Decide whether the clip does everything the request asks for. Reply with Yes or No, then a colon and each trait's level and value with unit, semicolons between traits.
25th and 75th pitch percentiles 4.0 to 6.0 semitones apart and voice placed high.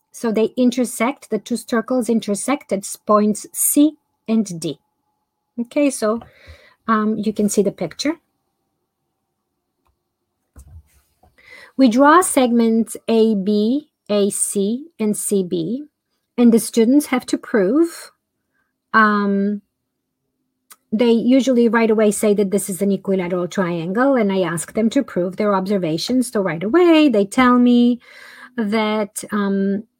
Yes: average, 4.3 semitones; high, 220 Hz